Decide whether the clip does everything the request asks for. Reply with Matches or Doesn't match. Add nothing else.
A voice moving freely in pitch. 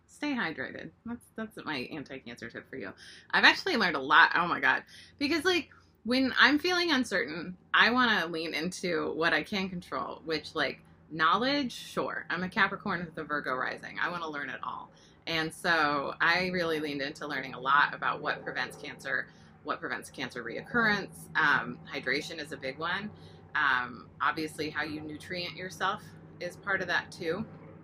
Matches